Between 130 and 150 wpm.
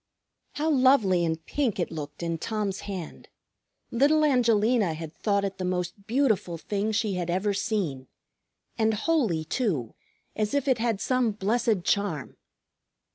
Yes: average, 145 wpm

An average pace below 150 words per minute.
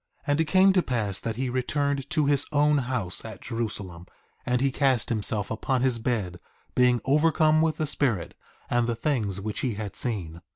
No: average, 195 wpm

